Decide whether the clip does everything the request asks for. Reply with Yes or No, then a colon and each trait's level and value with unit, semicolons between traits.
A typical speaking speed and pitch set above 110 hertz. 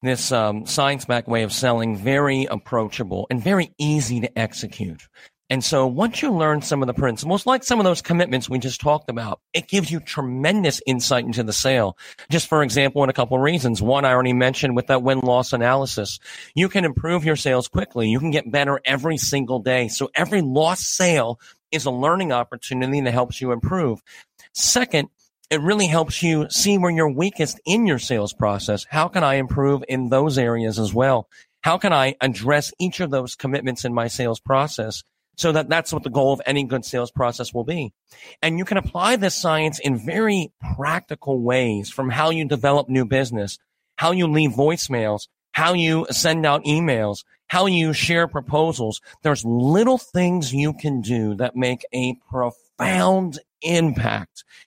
Yes: average, 185 wpm; low, 135 Hz